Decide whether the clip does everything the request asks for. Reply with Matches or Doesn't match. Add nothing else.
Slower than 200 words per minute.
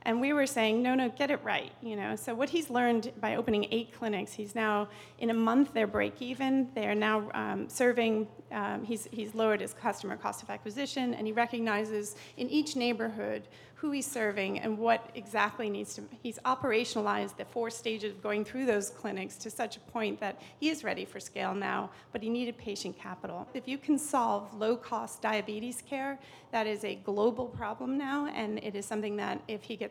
Doesn't match